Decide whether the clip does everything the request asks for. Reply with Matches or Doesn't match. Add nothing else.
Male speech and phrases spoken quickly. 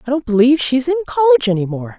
Doesn't match